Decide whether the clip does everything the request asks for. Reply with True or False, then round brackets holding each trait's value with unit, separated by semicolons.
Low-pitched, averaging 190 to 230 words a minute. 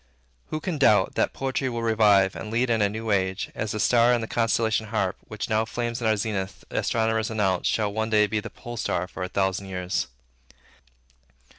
True (110 Hz; 200 wpm)